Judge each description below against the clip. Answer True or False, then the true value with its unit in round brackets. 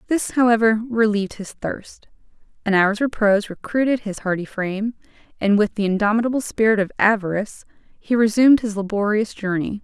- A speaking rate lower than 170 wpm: True (145 wpm)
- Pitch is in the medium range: False (215 Hz)